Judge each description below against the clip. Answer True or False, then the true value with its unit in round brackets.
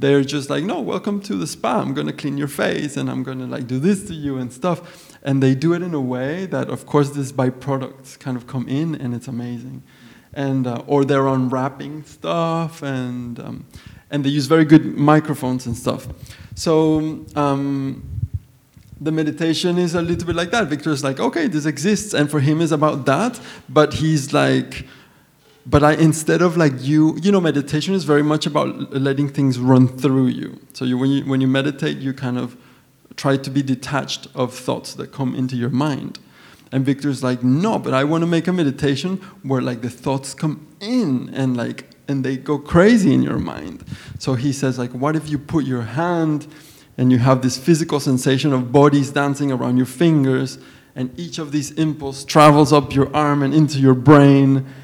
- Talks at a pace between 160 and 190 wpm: False (200 wpm)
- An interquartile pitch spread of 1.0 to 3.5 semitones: True (2.8 semitones)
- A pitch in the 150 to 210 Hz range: False (140 Hz)